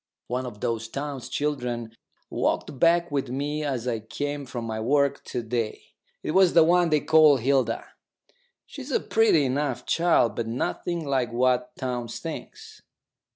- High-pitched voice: No, low, 135 Hz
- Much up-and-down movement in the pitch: No, average, 3.8 semitones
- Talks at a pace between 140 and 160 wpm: Yes, average, 155 wpm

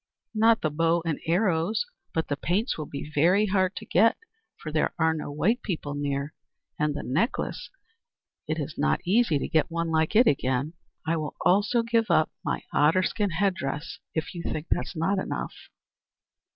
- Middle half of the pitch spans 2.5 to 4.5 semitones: No, average, 4.9 semitones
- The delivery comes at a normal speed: Yes, average, 185 wpm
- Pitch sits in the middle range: Yes, medium, 165 Hz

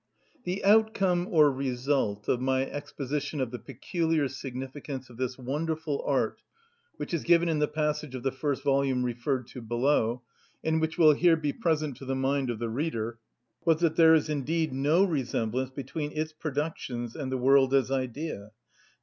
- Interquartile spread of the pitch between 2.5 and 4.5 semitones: Yes, average, 3.5 semitones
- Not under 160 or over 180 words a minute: Yes, average, 175 wpm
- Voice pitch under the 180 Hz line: Yes, medium, 140 Hz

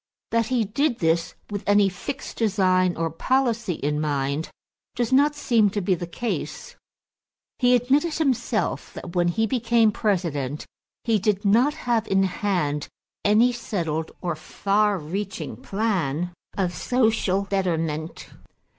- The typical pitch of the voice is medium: No, high, 200 Hz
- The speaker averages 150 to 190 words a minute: No, slow, 135 wpm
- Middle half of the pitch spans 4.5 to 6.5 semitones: Yes, average, 5.2 semitones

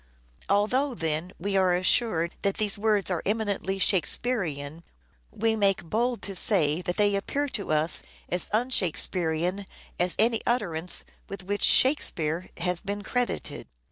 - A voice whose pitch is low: No, high, 195 Hz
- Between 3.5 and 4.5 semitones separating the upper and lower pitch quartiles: Yes, average, 3.9 semitones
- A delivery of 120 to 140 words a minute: No, average, 150 wpm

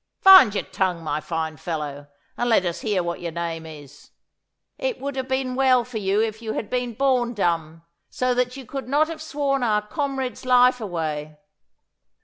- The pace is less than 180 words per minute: No, average, 185 wpm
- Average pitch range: No, wide, 7.6 semitones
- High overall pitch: Yes, high, 225 Hz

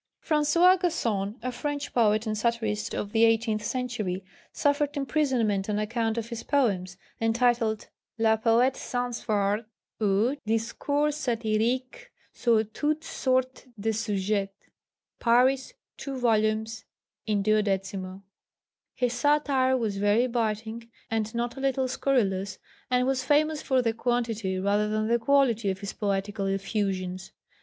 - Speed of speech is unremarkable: No, slow, 130 wpm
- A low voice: No, high, 225 Hz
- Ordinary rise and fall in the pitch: Yes, average, 3.5 semitones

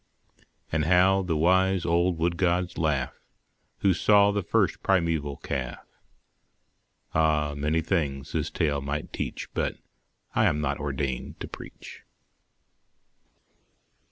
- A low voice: Yes, very low, 80 Hz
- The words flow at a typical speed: No, slow, 120 wpm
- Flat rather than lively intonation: No, average, 3.7 semitones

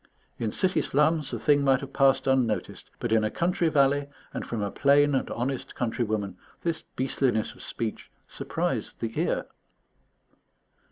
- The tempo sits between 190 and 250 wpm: No, average, 155 wpm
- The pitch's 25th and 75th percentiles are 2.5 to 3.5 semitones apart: No, average, 4.0 semitones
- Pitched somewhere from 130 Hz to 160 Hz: Yes, low, 135 Hz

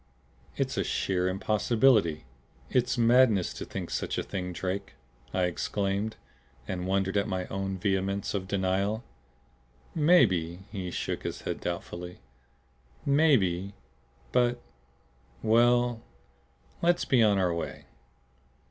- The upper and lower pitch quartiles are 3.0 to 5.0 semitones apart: Yes, average, 4.1 semitones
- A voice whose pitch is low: Yes, low, 100 Hz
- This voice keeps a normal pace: No, slow, 115 wpm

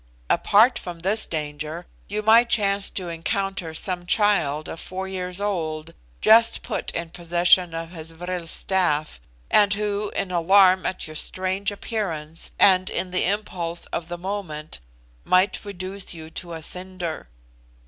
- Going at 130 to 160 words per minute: Yes, average, 150 wpm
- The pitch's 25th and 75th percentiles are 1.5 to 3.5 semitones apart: Yes, average, 3.1 semitones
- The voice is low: No, medium, 180 Hz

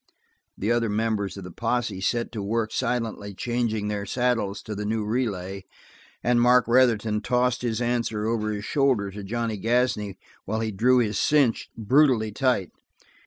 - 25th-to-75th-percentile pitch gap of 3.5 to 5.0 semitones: No, average, 2.8 semitones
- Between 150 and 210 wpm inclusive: Yes, average, 165 wpm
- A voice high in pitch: No, low, 110 Hz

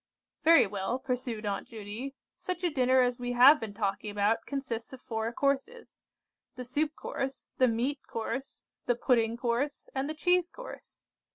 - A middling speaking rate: Yes, average, 165 wpm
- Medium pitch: No, very high, 250 Hz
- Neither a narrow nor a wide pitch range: Yes, average, 3.7 semitones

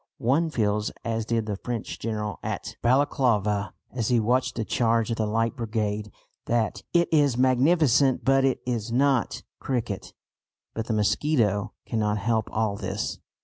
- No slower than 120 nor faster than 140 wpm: No, average, 150 wpm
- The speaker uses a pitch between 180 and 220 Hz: No, low, 115 Hz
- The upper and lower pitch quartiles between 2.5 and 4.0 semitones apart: Yes, average, 3.3 semitones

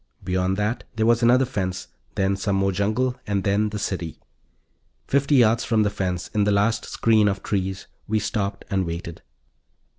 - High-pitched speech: No, low, 105 Hz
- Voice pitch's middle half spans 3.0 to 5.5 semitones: No, narrow, 2.5 semitones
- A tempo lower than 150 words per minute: No, average, 175 wpm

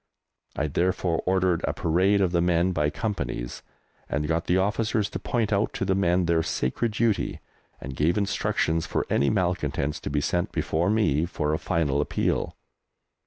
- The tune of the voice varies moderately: Yes, average, 4.3 semitones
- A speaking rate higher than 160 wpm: Yes, average, 170 wpm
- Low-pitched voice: Yes, very low, 85 Hz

